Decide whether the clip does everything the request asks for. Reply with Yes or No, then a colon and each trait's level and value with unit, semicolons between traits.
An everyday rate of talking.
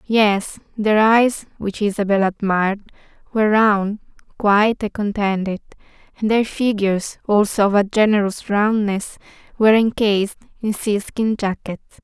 No: slow, 120 wpm